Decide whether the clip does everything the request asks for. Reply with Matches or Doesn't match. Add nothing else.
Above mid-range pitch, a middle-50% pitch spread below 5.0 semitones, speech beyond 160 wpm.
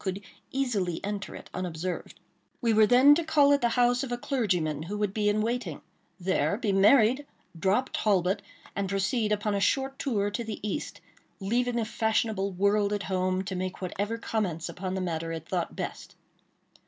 Matches